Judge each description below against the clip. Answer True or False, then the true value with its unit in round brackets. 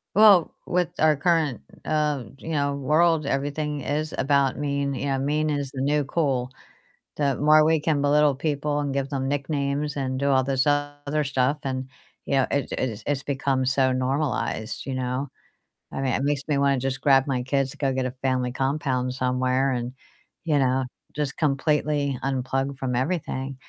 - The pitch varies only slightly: True (2.0 semitones)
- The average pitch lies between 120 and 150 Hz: True (140 Hz)